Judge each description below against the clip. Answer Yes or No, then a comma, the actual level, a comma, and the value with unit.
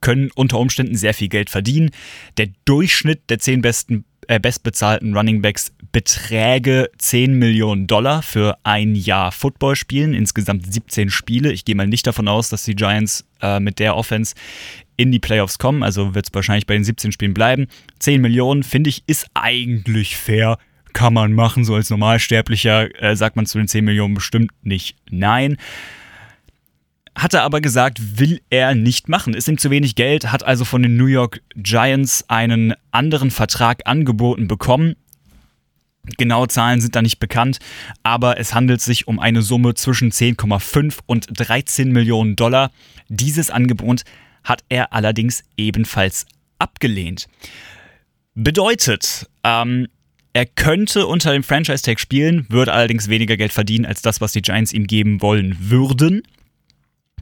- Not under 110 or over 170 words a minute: Yes, average, 155 wpm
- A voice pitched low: Yes, low, 115 Hz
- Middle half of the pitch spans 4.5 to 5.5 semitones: No, average, 3.1 semitones